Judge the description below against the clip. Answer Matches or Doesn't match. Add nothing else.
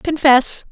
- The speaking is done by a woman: Matches